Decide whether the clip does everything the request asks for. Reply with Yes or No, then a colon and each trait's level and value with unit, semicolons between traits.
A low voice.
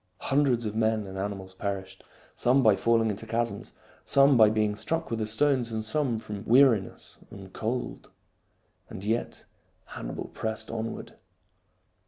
Yes: low, 110 Hz